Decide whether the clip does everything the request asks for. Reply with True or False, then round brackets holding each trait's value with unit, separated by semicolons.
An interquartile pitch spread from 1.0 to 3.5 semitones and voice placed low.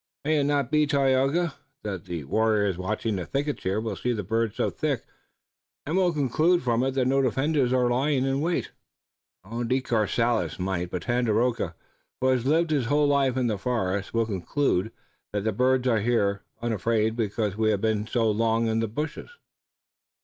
False (4.2 semitones; 120 Hz)